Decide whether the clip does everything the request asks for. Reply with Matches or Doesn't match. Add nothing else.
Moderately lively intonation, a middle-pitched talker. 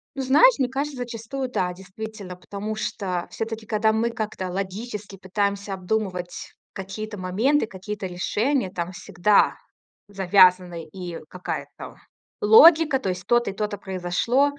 Doesn't match